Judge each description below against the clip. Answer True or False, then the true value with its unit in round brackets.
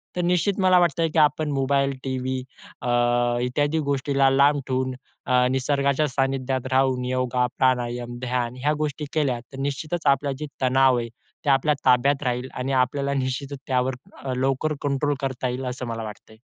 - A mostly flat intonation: True (2.0 semitones)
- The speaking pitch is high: False (135 Hz)